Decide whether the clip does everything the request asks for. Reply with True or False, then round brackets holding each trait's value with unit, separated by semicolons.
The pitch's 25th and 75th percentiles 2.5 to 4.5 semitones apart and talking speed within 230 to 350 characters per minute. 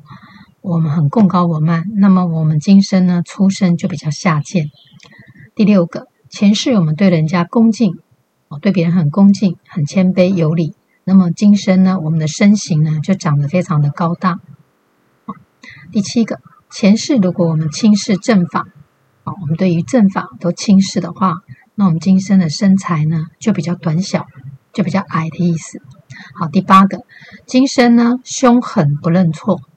True (3.6 semitones; 245 characters per minute)